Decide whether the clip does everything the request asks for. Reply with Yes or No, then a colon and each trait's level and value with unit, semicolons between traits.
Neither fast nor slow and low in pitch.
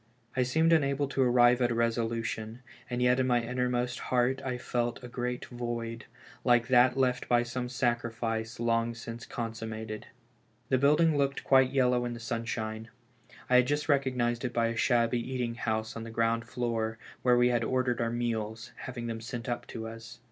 Yes: average, 185 wpm; low, 120 Hz